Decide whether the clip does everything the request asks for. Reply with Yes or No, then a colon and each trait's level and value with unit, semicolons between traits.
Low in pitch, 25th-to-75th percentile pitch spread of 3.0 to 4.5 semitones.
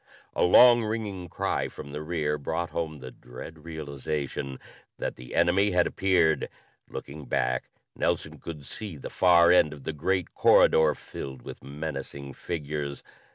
Yes: very low, 80 Hz; average, 3.7 semitones